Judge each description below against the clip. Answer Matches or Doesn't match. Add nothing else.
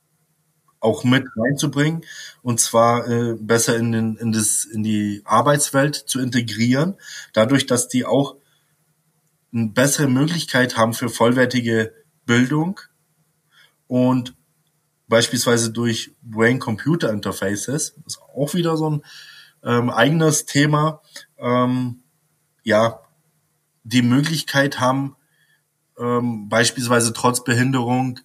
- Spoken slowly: Matches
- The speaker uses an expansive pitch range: Doesn't match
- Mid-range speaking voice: Doesn't match